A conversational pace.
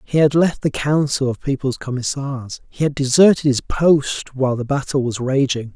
Yes: average, 190 wpm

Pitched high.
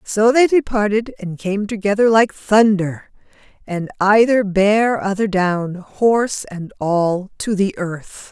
Yes: high, 205 Hz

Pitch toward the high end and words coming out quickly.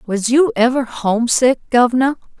No: high, 245 Hz; slow, 125 wpm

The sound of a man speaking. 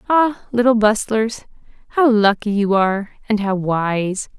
No: female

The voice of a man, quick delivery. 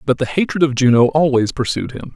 Yes: male; fast, 220 wpm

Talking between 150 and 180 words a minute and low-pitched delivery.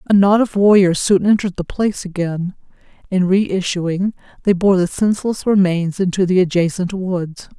No: average, 160 wpm; high, 190 Hz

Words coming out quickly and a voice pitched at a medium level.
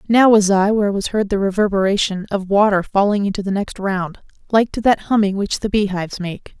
No: fast, 210 wpm; high, 200 Hz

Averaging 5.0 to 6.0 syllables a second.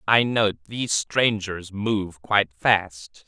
No: 3.3 syllables/s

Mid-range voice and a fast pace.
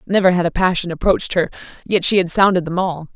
Yes: medium, 180 Hz; fast, 230 wpm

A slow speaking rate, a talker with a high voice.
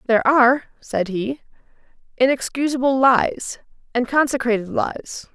Yes: slow, 100 wpm; very high, 250 Hz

